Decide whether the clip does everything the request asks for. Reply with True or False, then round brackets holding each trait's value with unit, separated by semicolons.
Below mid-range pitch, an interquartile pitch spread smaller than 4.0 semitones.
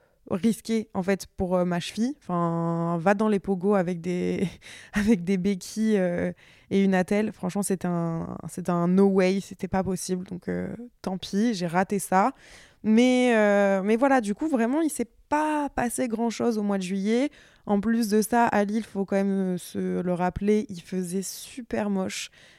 False (195 Hz; 3.4 semitones)